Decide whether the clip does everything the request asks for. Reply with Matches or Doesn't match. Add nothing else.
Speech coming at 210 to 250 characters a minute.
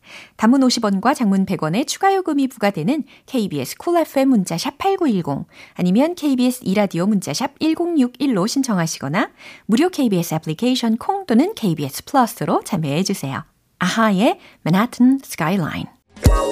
Doesn't match